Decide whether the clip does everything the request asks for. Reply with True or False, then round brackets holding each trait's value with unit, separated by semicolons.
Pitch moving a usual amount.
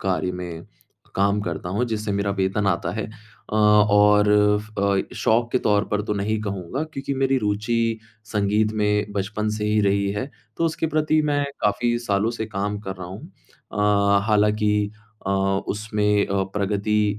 False (1.3 semitones)